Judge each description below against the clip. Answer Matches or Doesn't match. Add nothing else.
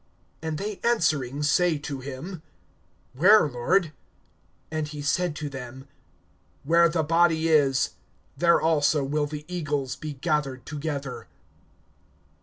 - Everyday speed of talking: Doesn't match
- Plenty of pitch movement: Doesn't match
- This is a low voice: Doesn't match